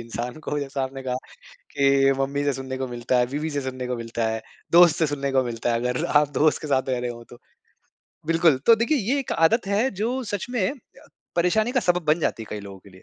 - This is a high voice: No, medium, 140 Hz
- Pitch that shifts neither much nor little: No, wide, 5.7 semitones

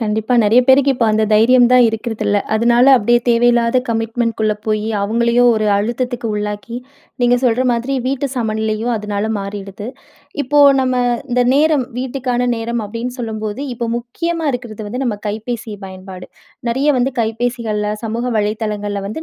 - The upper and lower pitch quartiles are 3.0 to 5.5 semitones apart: No, narrow, 2.4 semitones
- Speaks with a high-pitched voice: Yes, high, 230 Hz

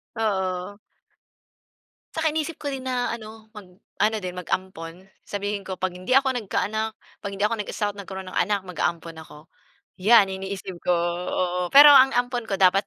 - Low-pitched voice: No, high, 205 Hz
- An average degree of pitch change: Yes, average, 3.8 semitones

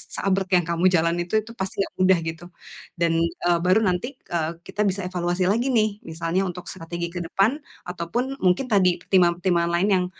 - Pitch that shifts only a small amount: Yes, narrow, 2.0 semitones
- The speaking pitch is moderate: Yes, medium, 180 Hz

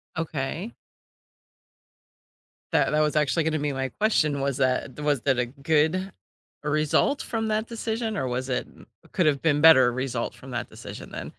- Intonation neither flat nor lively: Yes, average, 3.7 semitones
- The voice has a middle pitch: Yes, medium, 150 Hz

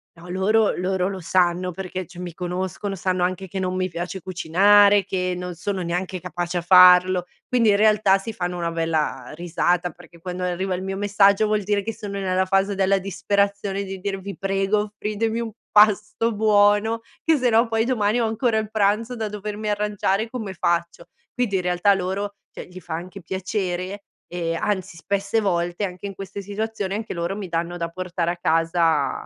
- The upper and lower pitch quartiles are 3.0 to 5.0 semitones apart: No, narrow, 2.5 semitones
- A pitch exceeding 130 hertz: Yes, high, 190 Hz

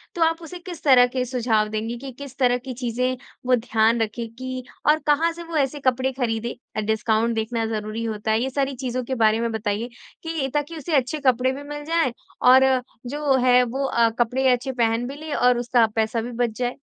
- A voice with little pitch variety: No, average, 3.1 semitones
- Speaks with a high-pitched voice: Yes, very high, 250 Hz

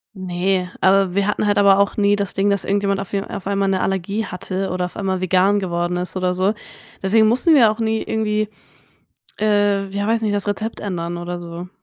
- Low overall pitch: No, high, 195 Hz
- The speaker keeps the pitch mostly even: Yes, narrow, 2.0 semitones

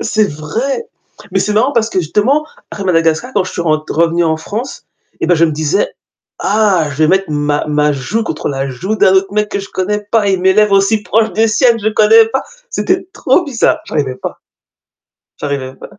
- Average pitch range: No, wide, 5.8 semitones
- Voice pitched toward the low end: No, high, 195 Hz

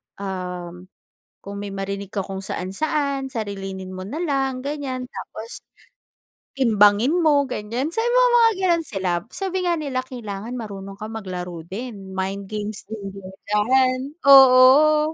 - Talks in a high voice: Yes, high, 220 Hz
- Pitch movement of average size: No, wide, 5.7 semitones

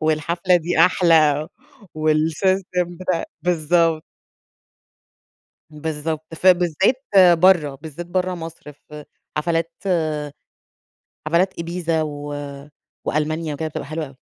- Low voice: No, medium, 160 Hz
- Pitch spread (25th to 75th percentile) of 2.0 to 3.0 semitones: Yes, narrow, 2.4 semitones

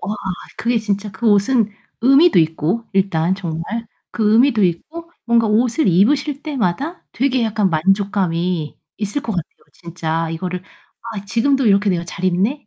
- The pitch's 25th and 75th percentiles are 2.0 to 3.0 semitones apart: No, average, 5.2 semitones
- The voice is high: Yes, high, 205 Hz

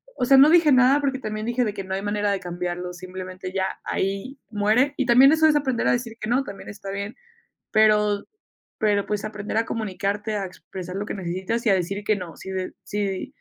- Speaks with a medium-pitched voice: No, high, 205 Hz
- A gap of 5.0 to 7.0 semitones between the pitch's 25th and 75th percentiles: No, average, 3.8 semitones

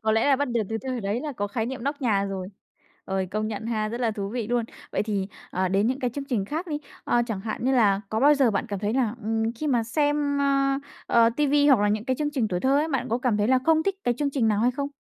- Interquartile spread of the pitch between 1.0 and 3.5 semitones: No, average, 4.5 semitones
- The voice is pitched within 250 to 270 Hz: No, high, 235 Hz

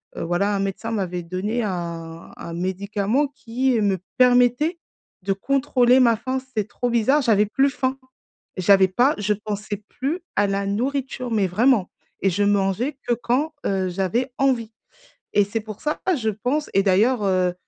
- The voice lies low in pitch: No, high, 215 Hz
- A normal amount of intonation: Yes, average, 4.6 semitones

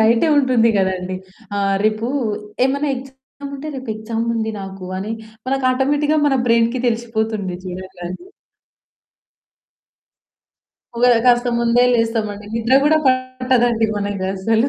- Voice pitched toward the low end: No, high, 230 Hz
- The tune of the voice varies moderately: Yes, average, 3.9 semitones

